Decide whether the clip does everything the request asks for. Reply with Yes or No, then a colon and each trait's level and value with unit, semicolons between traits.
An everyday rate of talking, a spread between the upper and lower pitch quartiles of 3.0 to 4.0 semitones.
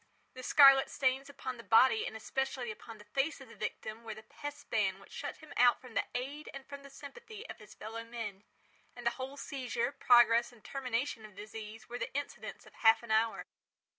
No: fast, 215 wpm; average, 3.6 semitones